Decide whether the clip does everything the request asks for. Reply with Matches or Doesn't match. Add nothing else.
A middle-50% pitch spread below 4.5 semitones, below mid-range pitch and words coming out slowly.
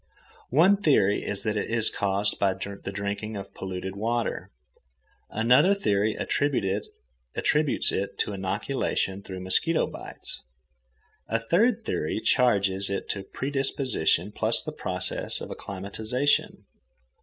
Doesn't match